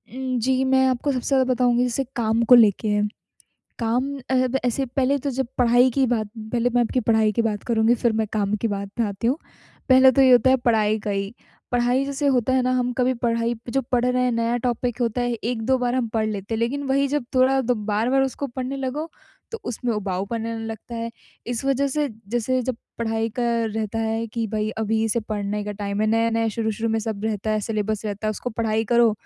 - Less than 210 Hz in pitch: No, high, 235 Hz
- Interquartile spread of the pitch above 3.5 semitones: No, average, 2.7 semitones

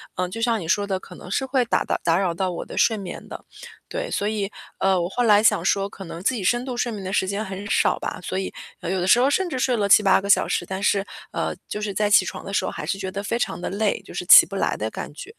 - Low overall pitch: No, high, 200 Hz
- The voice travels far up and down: No, average, 3.2 semitones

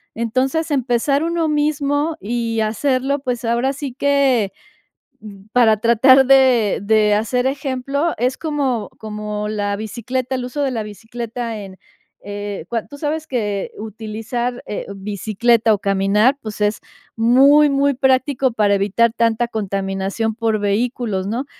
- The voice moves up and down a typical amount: Yes, average, 4.0 semitones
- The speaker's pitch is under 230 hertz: No, high, 235 Hz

